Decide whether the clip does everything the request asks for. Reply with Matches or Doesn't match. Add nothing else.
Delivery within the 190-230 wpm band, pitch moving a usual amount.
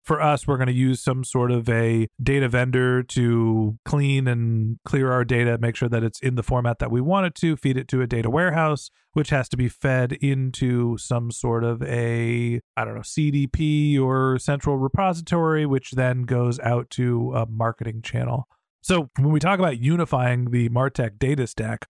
Matches